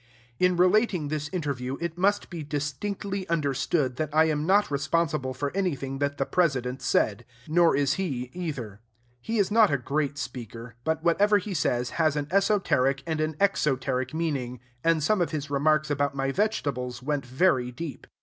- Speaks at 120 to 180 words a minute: Yes, average, 170 wpm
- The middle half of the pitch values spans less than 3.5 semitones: No, average, 4.5 semitones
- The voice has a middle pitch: Yes, medium, 150 Hz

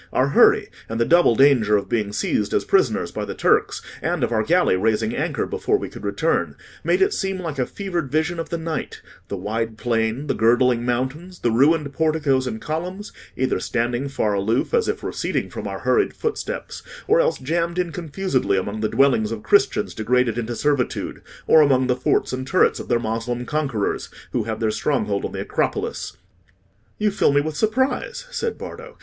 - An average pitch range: No, wide, 6.8 semitones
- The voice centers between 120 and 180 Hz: Yes, low, 135 Hz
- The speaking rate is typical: Yes, average, 190 wpm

